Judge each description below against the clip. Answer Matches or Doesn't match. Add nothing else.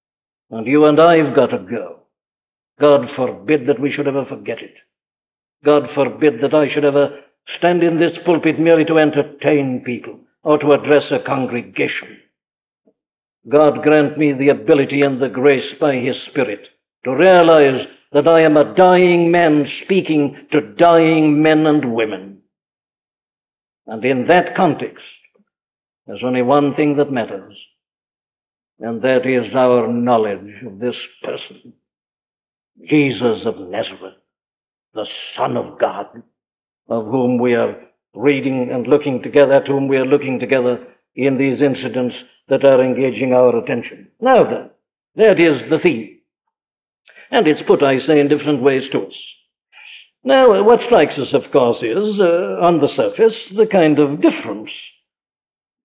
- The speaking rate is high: Doesn't match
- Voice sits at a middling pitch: Matches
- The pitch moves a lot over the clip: Doesn't match